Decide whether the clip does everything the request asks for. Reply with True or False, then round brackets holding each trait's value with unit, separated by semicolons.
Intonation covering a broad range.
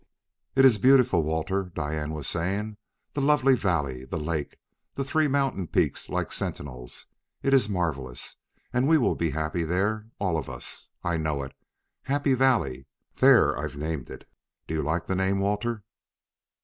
True (7.8 semitones)